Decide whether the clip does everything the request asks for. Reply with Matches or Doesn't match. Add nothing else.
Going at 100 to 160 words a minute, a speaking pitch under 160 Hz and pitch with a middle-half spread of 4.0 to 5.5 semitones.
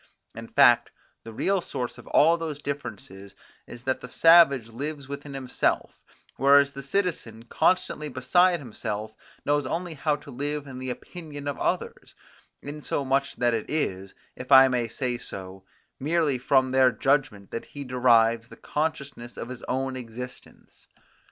Doesn't match